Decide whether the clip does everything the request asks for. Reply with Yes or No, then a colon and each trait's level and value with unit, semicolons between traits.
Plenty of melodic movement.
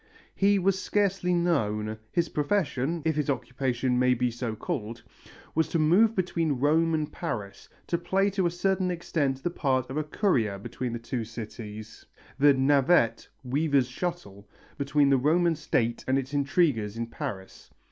Yes: wide, 6.1 semitones